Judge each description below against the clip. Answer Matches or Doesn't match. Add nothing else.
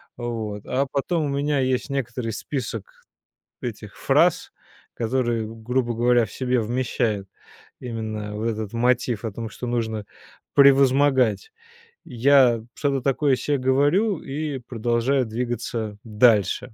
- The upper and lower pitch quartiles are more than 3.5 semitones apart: Doesn't match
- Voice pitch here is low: Matches